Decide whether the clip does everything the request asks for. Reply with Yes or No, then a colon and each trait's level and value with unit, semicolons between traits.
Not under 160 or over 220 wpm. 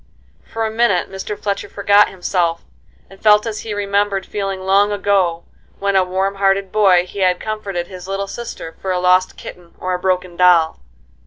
Yes: average, 180 wpm